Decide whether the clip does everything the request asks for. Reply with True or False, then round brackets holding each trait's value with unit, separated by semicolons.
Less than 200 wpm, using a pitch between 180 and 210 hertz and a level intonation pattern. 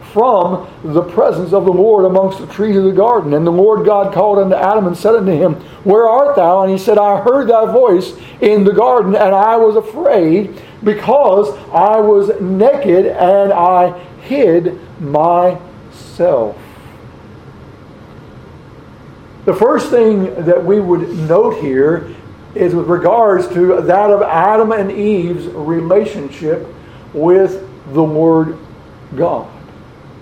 False (140 wpm; 190 Hz; 3.1 semitones)